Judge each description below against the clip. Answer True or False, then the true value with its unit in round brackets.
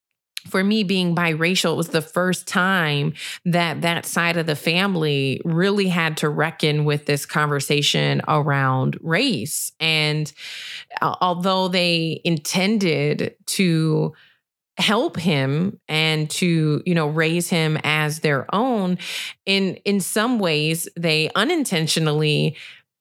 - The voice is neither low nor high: True (165 Hz)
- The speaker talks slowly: True (120 wpm)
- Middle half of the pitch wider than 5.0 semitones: False (3.3 semitones)